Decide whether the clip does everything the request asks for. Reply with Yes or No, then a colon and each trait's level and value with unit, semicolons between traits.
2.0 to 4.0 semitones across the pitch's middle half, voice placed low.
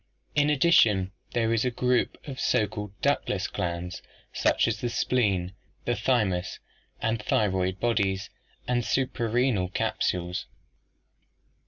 No: average, 4.5 semitones; low, 110 Hz